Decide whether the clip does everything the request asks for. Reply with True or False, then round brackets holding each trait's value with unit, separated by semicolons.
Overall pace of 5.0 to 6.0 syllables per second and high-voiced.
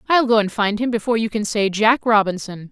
True (5.9 syllables/s; 220 Hz)